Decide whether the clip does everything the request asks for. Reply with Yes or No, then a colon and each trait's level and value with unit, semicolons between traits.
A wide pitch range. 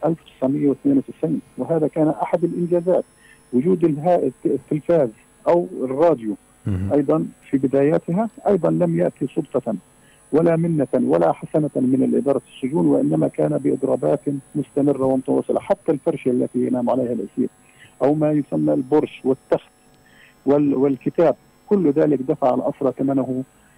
No: average, 4.0 semitones